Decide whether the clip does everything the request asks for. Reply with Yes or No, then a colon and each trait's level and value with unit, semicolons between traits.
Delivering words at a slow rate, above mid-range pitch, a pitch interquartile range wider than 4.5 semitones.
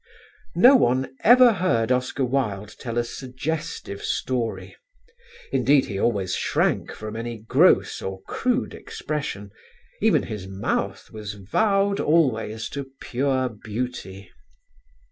No: slow, 115 wpm; low, 125 Hz; average, 5.3 semitones